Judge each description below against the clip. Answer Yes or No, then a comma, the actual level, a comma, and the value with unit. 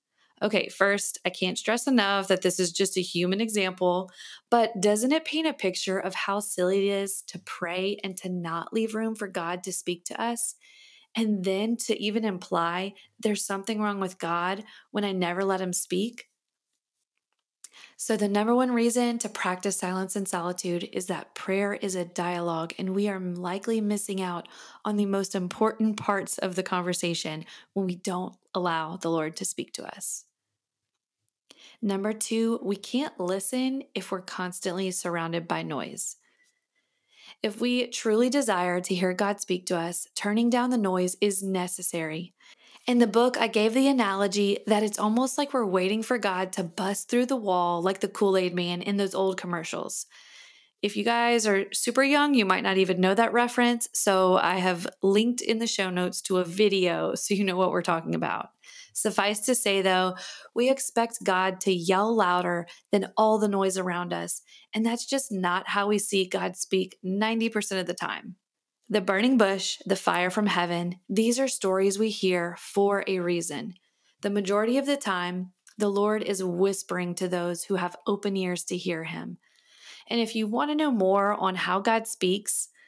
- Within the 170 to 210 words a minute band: Yes, average, 185 wpm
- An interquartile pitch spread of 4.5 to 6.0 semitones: No, average, 3.3 semitones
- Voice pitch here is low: No, high, 195 Hz